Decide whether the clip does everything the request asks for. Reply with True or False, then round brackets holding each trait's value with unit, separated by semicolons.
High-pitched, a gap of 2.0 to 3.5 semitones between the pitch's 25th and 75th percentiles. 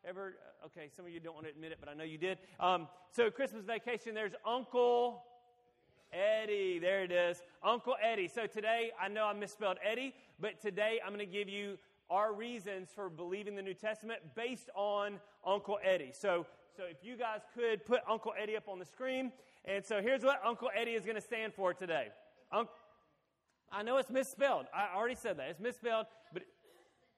False (210 Hz; 4.0 semitones)